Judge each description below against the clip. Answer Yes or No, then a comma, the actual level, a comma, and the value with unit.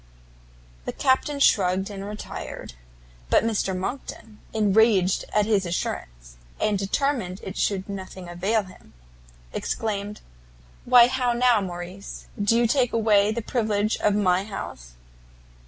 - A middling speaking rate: No, slow, 125 wpm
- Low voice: No, high, 205 Hz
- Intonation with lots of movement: No, average, 3.2 semitones